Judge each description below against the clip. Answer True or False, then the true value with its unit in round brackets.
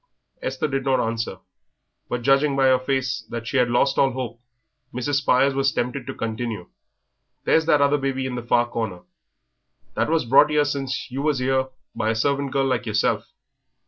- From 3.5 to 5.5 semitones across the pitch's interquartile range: False (2.5 semitones)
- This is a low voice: True (130 Hz)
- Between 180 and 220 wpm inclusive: True (185 wpm)